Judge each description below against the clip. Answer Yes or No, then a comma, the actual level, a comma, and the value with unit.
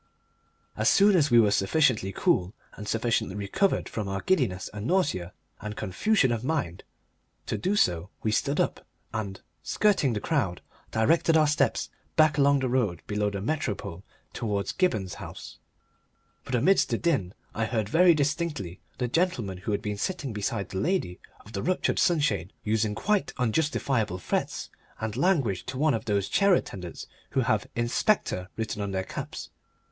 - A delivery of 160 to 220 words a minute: Yes, average, 165 wpm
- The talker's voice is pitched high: No, low, 115 Hz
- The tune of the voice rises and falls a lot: Yes, wide, 7.3 semitones